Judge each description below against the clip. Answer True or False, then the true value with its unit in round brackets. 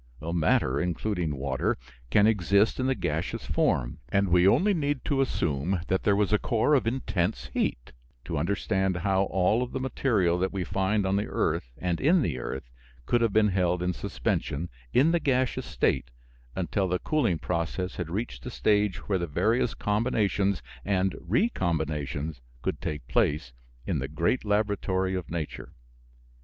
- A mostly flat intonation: False (4.3 semitones)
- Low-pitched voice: True (95 Hz)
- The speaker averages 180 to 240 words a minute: False (165 wpm)